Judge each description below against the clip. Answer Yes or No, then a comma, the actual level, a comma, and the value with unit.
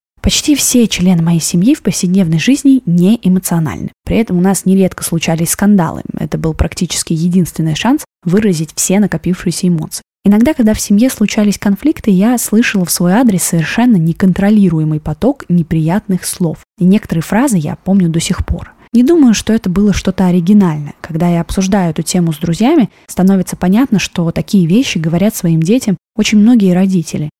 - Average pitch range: Yes, average, 3.9 semitones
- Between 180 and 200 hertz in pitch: Yes, high, 190 Hz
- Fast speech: Yes, fast, 165 wpm